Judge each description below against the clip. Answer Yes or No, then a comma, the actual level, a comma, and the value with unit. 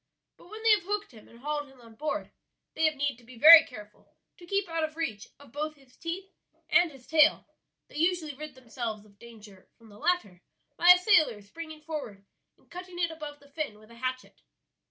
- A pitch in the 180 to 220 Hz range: No, very high, 295 Hz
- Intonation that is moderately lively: No, wide, 6.1 semitones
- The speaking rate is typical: No, fast, 215 wpm